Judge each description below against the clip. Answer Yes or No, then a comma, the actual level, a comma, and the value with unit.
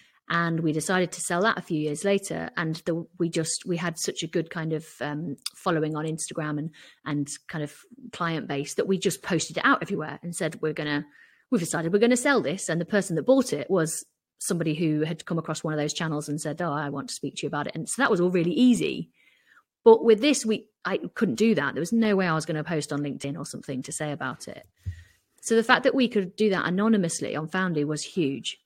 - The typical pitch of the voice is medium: Yes, medium, 165 Hz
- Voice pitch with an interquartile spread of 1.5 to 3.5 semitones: No, average, 4.6 semitones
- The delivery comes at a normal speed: No, fast, 255 wpm